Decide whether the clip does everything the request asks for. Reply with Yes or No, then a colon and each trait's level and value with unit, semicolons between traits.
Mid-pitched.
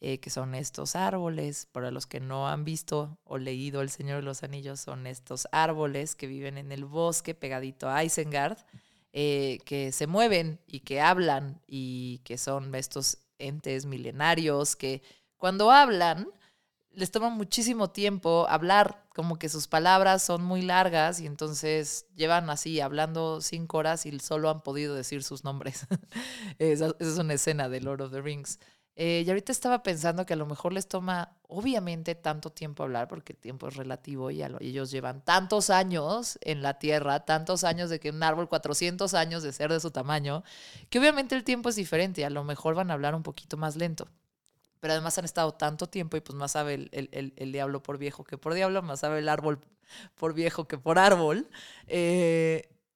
Yes: medium, 155 Hz